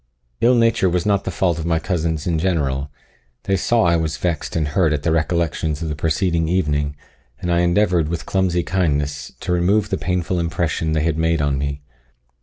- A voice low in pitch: Yes, very low, 85 Hz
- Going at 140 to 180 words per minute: No, average, 195 wpm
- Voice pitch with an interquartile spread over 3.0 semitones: No, average, 2.7 semitones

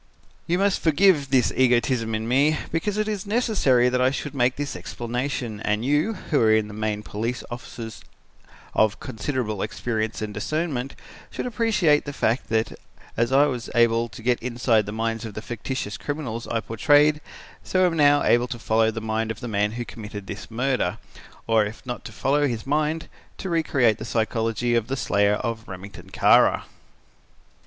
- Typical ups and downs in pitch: Yes, average, 4.6 semitones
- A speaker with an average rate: Yes, average, 180 wpm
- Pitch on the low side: Yes, low, 120 Hz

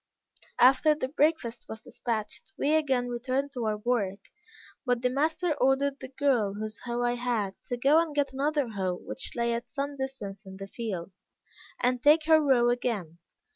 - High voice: Yes, very high, 250 Hz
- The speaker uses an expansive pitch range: No, average, 3.9 semitones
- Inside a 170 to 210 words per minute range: Yes, average, 175 wpm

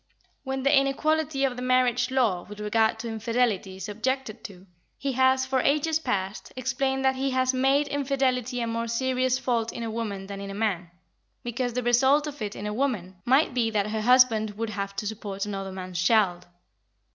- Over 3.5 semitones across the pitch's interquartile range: Yes, average, 4.0 semitones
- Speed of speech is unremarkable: Yes, average, 195 wpm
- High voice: Yes, high, 240 Hz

